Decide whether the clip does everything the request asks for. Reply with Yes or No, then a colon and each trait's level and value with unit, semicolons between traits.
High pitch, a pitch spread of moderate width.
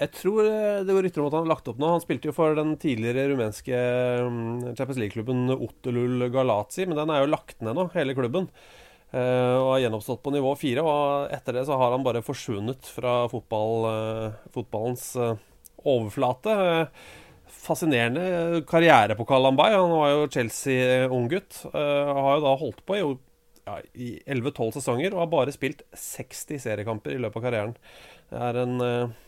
No: low, 130 Hz; average, 3.4 semitones